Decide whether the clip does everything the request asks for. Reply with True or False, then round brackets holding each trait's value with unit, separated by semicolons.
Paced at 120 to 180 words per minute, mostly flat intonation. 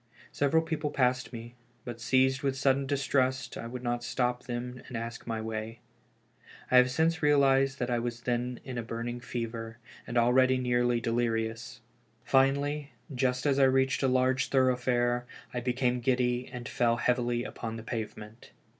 True (165 wpm; 1.8 semitones)